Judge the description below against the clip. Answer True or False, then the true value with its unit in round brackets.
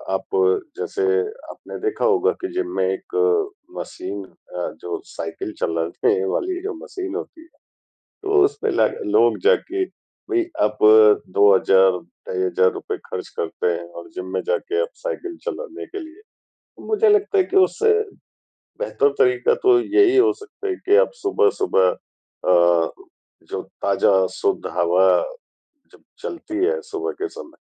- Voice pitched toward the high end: True (380 Hz)